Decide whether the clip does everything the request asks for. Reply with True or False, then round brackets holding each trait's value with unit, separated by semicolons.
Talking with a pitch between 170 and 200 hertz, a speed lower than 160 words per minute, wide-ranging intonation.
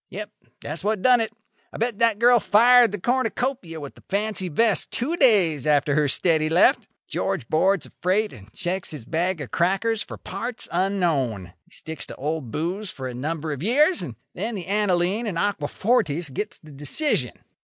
False (185 Hz; 185 wpm; 6.2 semitones)